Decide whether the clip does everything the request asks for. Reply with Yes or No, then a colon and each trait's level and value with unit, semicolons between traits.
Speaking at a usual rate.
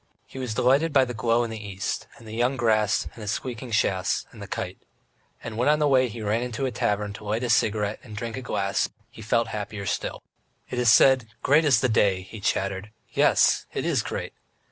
No: fast, 225 wpm